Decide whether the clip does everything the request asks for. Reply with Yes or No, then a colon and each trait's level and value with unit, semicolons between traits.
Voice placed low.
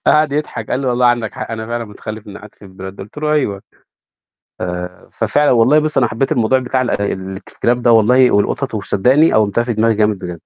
Yes: low, 115 Hz